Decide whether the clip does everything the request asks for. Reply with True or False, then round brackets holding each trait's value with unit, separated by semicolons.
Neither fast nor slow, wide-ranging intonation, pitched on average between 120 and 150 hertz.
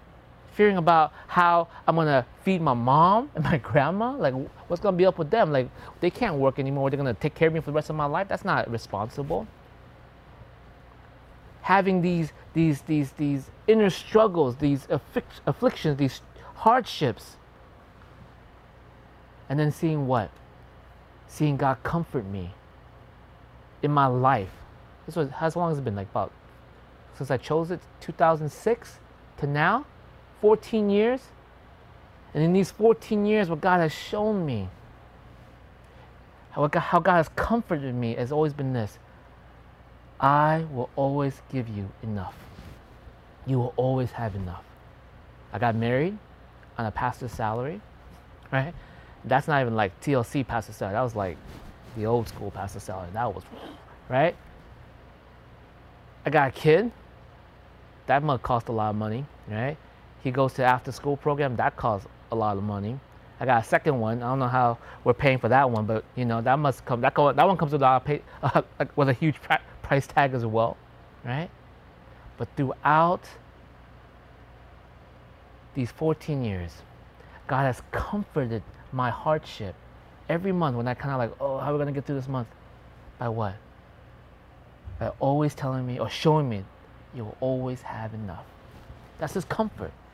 True (160 wpm; 5.7 semitones; 135 Hz)